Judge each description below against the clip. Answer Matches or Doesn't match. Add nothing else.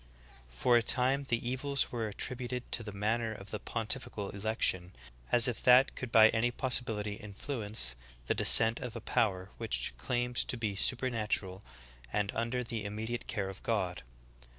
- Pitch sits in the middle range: Doesn't match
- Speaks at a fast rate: Doesn't match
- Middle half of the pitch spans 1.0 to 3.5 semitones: Matches